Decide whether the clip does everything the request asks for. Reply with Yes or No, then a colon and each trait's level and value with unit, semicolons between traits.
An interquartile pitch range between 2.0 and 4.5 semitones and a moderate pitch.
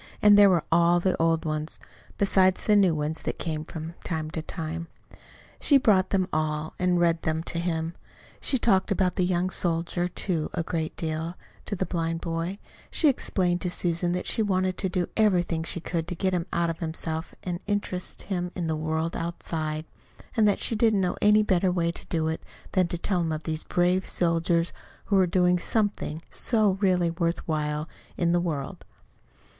Yes: narrow, 2.4 semitones; medium, 175 Hz